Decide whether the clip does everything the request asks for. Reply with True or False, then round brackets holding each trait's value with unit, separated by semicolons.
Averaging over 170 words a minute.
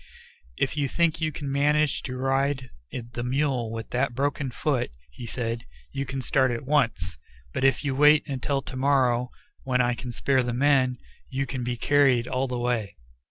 True (185 wpm)